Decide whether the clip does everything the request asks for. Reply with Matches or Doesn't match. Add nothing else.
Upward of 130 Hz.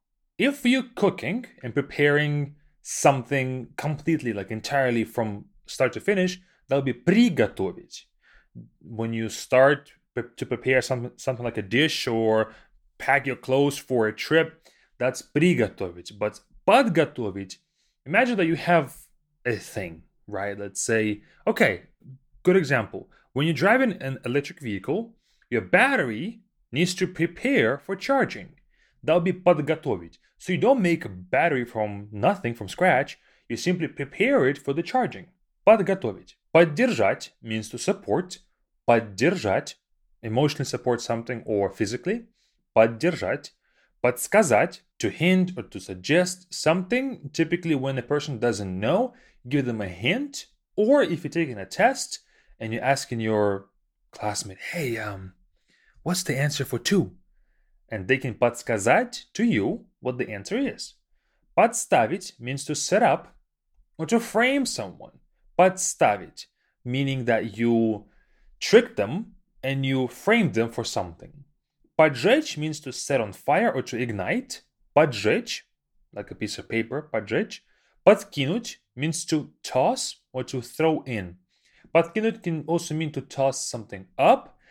Matches